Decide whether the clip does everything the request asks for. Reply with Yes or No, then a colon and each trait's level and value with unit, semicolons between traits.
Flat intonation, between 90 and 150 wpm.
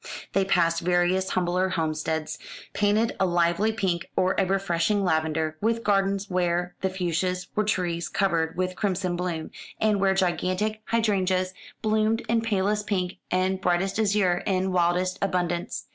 Yes: narrow, 2.2 semitones; average, 145 wpm